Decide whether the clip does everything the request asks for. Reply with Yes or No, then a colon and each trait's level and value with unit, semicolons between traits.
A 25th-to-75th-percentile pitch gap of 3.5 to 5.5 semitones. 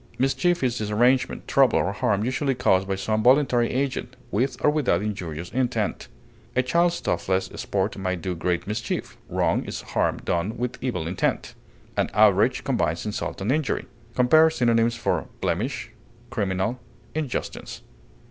Yes: average, 5.1 semitones